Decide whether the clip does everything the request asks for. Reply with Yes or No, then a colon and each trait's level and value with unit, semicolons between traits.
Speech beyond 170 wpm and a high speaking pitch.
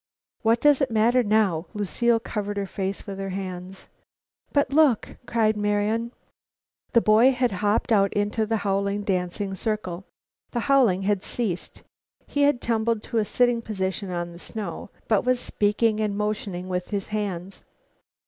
No: average, 160 wpm; high, 210 Hz